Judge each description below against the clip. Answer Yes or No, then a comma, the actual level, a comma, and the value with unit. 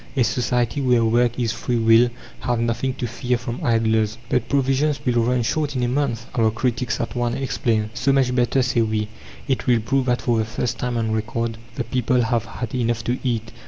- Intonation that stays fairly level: Yes, narrow, 1.8 semitones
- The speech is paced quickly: Yes, fast, 215 wpm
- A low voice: Yes, low, 120 Hz